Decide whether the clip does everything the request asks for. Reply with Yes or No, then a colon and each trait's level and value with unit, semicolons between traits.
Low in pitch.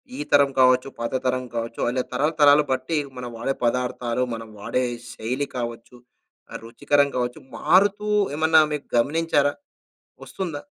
Yes: low, 130 Hz